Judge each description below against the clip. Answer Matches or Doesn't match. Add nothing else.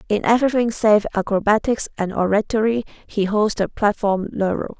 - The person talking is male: Doesn't match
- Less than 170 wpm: Matches